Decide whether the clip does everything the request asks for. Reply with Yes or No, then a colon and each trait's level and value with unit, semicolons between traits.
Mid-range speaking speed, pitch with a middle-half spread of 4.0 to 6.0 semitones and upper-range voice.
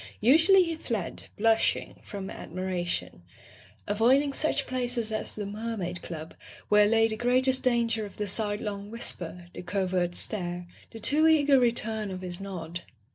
Yes: average, 150 wpm; average, 4.6 semitones; high, 215 Hz